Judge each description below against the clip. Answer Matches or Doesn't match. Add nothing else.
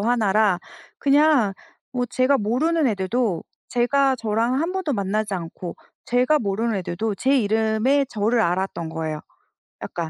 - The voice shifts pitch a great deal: Doesn't match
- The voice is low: Doesn't match